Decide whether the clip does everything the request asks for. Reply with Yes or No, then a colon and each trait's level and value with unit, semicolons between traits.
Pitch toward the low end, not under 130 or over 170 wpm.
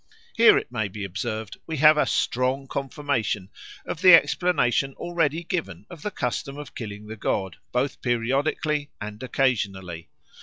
Yes: low, 130 Hz; average, 150 wpm